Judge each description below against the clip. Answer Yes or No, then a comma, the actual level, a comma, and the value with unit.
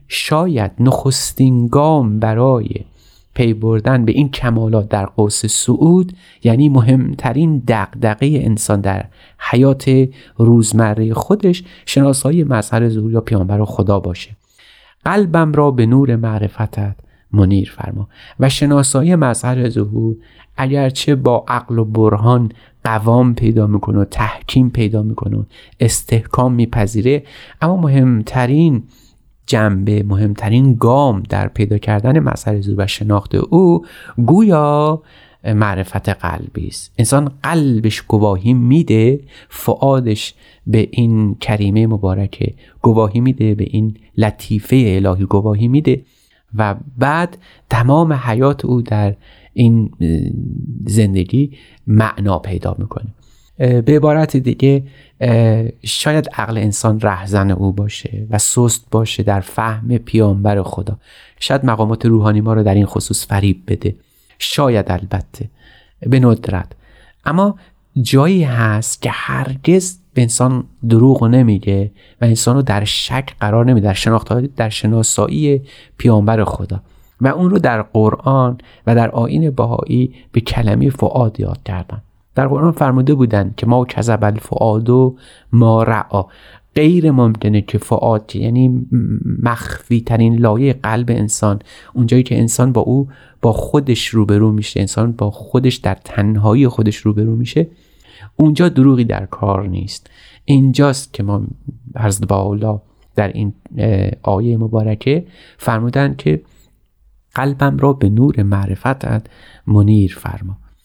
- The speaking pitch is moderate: No, low, 115 Hz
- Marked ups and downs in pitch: No, average, 3.8 semitones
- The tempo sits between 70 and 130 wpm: Yes, average, 120 wpm